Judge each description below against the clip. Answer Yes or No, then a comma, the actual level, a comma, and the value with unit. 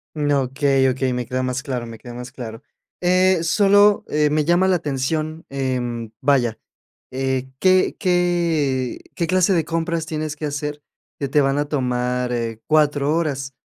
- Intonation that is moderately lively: Yes, average, 4.2 semitones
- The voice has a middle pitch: Yes, medium, 145 Hz